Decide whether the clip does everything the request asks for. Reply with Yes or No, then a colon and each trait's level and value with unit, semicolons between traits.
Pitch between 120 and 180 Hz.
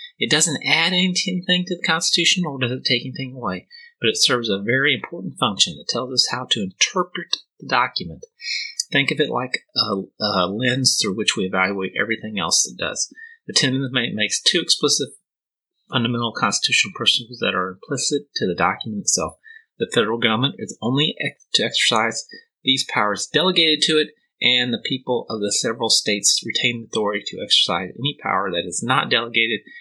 Yes: low, 135 Hz